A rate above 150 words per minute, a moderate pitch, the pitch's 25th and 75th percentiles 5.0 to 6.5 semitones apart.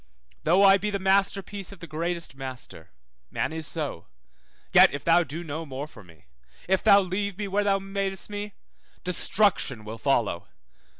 Yes: average, 170 wpm; medium, 175 Hz; wide, 5.6 semitones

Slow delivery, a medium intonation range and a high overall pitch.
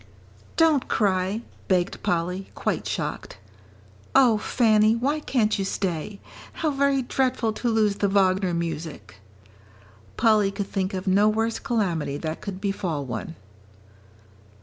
Yes: slow, 125 wpm; average, 3.8 semitones; high, 200 Hz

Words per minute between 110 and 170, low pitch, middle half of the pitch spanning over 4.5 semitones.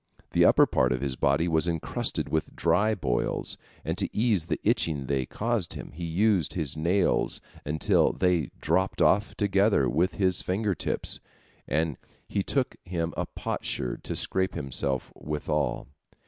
Yes: average, 150 wpm; very low, 85 Hz; average, 4.9 semitones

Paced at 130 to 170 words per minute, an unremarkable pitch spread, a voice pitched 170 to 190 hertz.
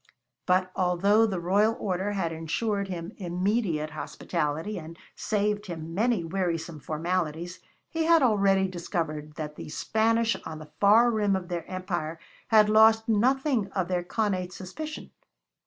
Yes: average, 140 wpm; average, 4.2 semitones; medium, 185 Hz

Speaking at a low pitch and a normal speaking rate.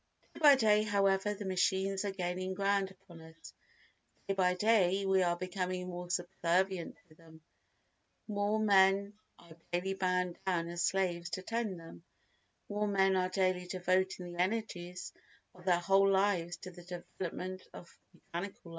No: medium, 185 Hz; average, 155 wpm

